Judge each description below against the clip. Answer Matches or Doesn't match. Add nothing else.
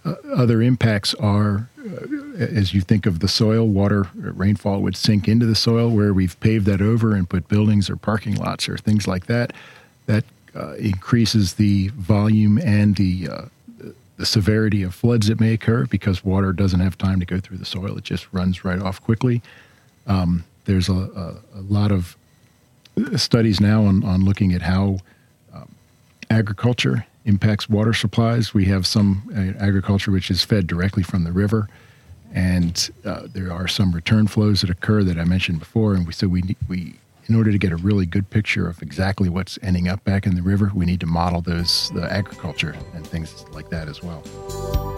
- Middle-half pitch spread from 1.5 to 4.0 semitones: Matches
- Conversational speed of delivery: Matches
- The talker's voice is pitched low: Matches